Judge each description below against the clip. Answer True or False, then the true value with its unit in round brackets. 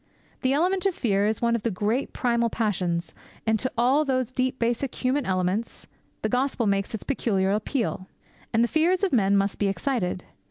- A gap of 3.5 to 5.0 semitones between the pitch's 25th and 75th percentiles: True (4.6 semitones)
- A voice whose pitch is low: False (235 Hz)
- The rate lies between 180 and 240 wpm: True (190 wpm)